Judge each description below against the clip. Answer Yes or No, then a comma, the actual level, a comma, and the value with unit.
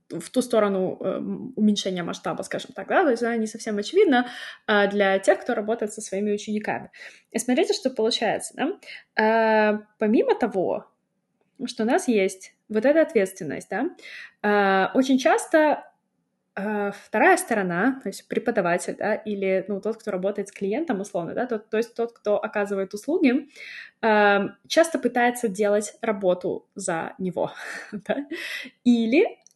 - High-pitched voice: Yes, high, 215 Hz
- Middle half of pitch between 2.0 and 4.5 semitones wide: Yes, average, 3.5 semitones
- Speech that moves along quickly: No, average, 140 wpm